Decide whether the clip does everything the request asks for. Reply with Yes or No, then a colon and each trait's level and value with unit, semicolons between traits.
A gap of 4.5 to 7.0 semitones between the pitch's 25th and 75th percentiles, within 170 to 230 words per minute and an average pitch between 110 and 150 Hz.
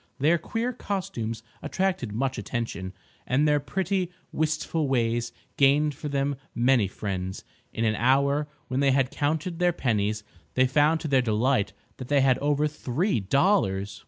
No: average, 4.8 semitones; average, 155 wpm; low, 135 Hz